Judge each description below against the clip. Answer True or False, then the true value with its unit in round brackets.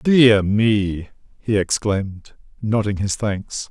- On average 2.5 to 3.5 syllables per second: True (3.3 syllables/s)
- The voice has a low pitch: True (105 Hz)